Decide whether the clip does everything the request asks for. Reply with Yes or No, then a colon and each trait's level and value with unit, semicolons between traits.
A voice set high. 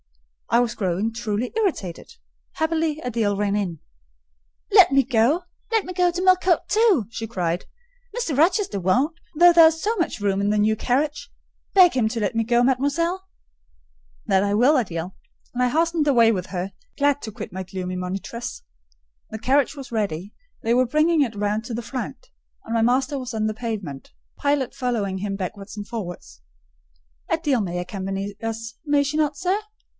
Yes: high, 235 Hz